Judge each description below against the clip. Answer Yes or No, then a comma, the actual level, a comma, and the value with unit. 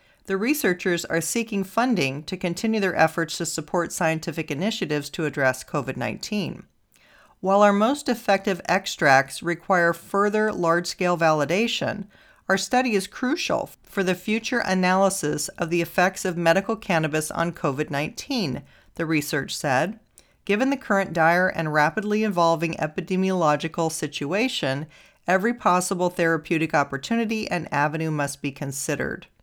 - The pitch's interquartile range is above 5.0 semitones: No, average, 4.1 semitones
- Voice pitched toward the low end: No, medium, 175 Hz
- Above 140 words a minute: No, slow, 135 wpm